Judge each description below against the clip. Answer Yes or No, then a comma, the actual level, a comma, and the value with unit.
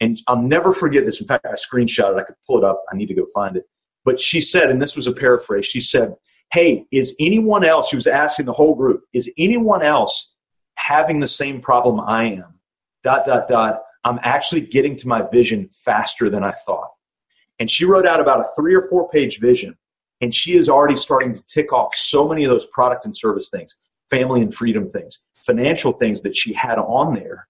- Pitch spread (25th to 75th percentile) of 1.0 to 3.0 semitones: No, average, 4.7 semitones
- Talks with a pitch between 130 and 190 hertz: Yes, low, 135 Hz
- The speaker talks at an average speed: No, fast, 220 wpm